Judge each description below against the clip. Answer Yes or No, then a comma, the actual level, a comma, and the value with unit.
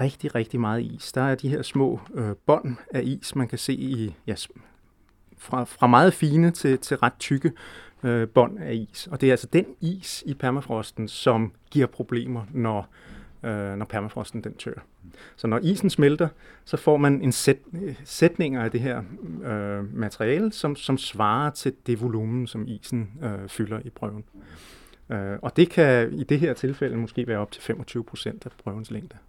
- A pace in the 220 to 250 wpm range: No, average, 185 wpm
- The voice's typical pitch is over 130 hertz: No, low, 125 Hz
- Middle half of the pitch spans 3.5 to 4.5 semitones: Yes, average, 4.1 semitones